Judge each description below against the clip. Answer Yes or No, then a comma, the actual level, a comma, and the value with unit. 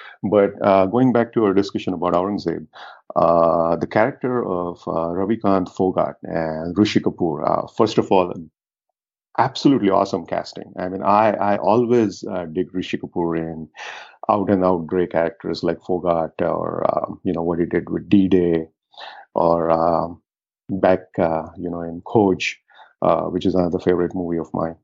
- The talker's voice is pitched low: Yes, very low, 90 Hz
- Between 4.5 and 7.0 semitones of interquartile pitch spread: No, average, 2.8 semitones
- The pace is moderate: Yes, average, 160 wpm